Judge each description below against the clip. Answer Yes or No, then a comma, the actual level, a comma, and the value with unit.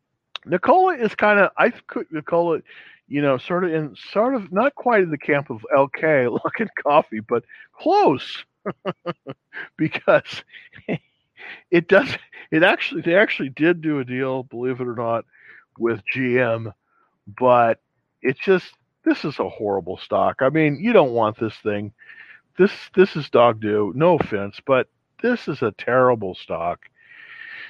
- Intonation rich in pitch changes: Yes, wide, 7.4 semitones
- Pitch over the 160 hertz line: No, medium, 140 Hz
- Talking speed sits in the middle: Yes, average, 150 wpm